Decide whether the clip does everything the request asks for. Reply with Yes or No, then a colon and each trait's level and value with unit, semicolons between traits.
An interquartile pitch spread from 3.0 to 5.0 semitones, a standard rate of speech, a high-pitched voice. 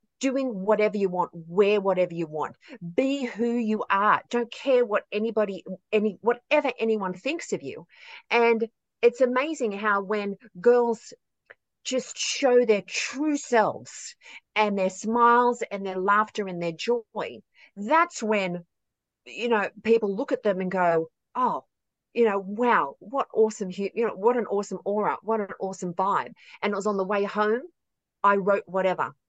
Yes: average, 3.3 semitones; average, 160 wpm; high, 215 Hz